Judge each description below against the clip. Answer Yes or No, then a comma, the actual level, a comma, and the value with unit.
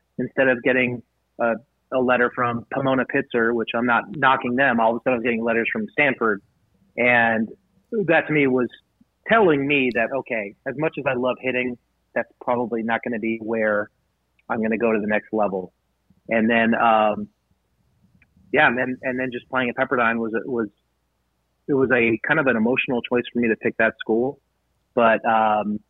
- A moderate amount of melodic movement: No, narrow, 2.3 semitones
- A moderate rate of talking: Yes, average, 195 wpm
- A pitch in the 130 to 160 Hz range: No, low, 120 Hz